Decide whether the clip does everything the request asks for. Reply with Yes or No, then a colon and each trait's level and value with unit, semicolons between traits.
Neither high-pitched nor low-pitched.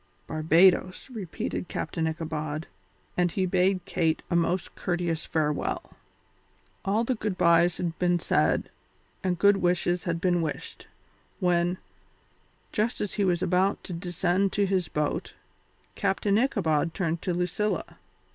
Yes: medium, 180 Hz